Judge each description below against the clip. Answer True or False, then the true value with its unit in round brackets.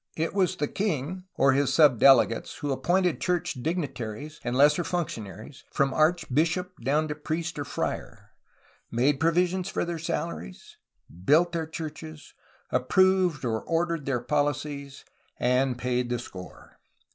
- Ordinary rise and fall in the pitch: True (4.5 semitones)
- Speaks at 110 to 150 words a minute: True (135 wpm)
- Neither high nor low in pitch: True (150 Hz)